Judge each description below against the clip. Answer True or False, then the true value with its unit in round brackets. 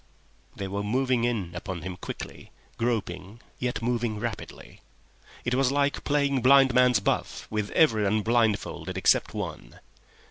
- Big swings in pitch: False (3.8 semitones)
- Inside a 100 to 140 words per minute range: True (135 wpm)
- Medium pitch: False (115 Hz)